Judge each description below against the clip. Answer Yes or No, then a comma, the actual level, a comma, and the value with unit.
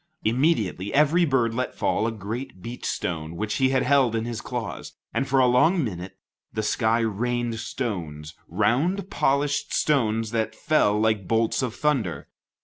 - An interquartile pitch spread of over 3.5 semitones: Yes, average, 3.9 semitones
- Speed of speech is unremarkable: Yes, average, 155 wpm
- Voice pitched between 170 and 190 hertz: No, low, 115 Hz